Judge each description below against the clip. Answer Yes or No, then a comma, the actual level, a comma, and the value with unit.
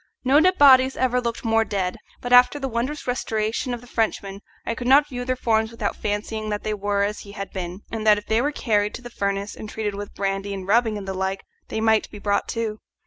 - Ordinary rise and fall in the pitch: Yes, average, 3.3 semitones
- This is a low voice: No, high, 220 Hz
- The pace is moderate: No, fast, 250 wpm